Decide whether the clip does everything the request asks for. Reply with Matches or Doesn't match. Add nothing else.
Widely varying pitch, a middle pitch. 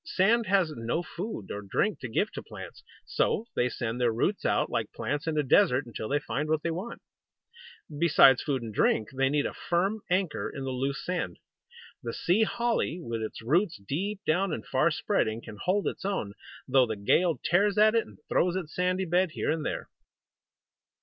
Matches